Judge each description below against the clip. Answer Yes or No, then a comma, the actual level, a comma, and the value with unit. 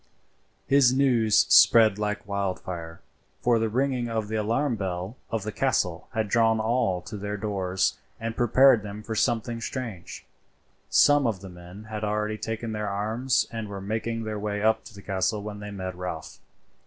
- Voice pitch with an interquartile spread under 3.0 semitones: Yes, narrow, 2.5 semitones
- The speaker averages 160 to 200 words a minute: Yes, average, 175 wpm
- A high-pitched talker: No, low, 110 Hz